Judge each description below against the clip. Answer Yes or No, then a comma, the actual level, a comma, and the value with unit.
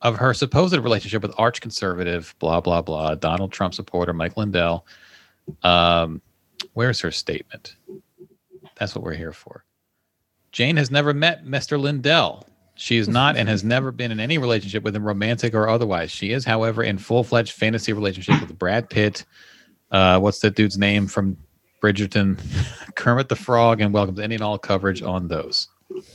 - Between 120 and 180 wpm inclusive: Yes, average, 170 wpm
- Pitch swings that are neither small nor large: Yes, average, 4.0 semitones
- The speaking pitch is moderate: No, low, 110 Hz